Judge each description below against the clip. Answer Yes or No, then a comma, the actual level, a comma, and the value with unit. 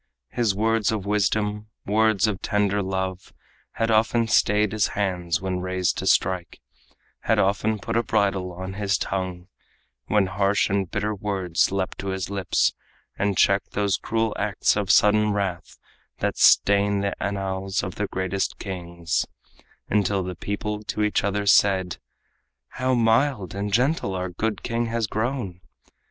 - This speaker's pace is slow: No, average, 150 wpm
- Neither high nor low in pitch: No, low, 100 Hz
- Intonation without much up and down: Yes, narrow, 2.0 semitones